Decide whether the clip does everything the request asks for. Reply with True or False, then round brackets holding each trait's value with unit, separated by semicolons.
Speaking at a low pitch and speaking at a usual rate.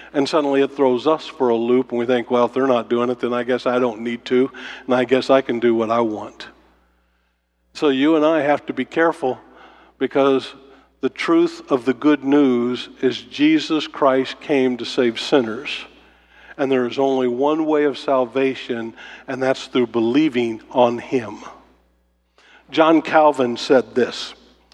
True (130 Hz; 175 wpm)